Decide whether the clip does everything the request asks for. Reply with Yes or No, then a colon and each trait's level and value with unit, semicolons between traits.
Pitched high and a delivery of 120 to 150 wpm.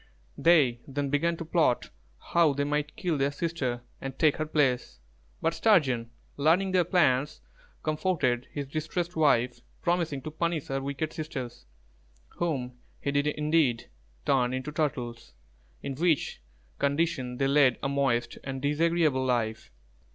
No: medium, 145 Hz; average, 140 wpm